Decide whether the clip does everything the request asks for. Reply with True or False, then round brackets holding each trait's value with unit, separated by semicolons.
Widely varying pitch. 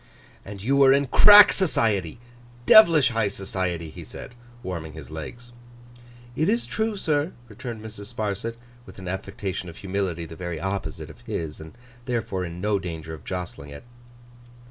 True (6.1 semitones)